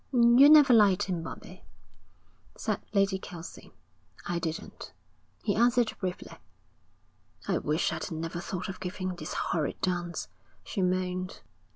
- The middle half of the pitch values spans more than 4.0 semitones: No, average, 3.2 semitones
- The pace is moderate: No, slow, 130 wpm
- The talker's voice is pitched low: No, medium, 185 Hz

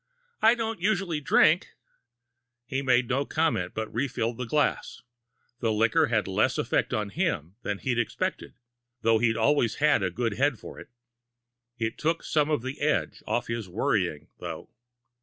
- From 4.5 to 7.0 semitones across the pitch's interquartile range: Yes, average, 5.1 semitones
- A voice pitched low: Yes, low, 120 Hz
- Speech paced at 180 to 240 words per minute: No, average, 160 wpm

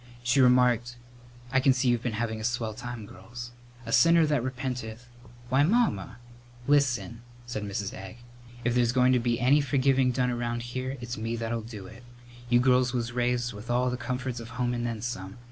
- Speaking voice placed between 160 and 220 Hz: No, low, 120 Hz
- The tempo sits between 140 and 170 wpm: No, average, 195 wpm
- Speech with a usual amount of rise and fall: No, narrow, 1.5 semitones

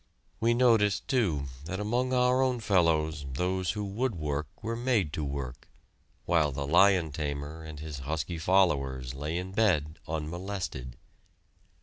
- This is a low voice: Yes, very low, 85 Hz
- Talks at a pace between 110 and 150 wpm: Yes, average, 140 wpm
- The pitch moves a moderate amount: No, wide, 5.8 semitones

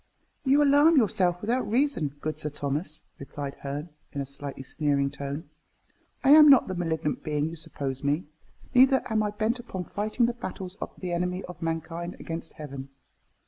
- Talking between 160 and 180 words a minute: Yes, average, 175 wpm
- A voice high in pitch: No, medium, 170 Hz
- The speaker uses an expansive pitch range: Yes, wide, 7.2 semitones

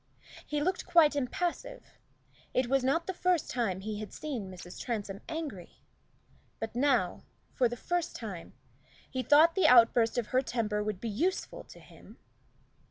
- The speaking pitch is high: Yes, very high, 250 Hz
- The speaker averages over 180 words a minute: No, average, 160 wpm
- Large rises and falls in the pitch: Yes, wide, 6.5 semitones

